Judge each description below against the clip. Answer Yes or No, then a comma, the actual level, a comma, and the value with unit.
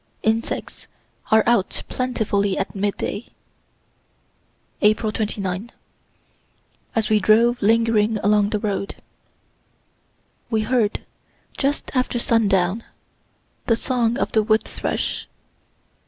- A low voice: No, high, 215 Hz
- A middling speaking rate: No, slow, 95 wpm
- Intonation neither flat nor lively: No, narrow, 2.0 semitones